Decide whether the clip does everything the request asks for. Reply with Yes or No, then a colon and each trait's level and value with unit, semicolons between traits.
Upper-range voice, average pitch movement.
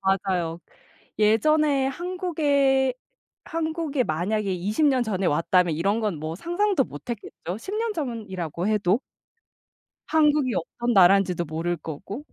No: high, 215 Hz; wide, 8.5 semitones